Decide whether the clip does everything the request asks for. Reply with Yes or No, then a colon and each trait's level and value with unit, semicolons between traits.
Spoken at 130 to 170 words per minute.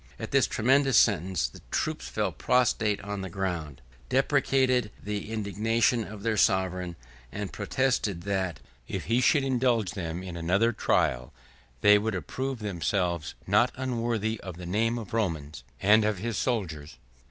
Yes: average, 150 wpm